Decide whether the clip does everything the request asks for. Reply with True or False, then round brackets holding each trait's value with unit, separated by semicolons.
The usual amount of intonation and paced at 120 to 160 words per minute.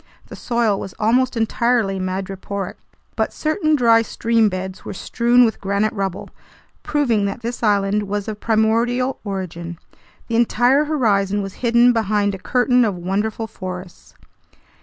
True (3.4 semitones; 140 wpm)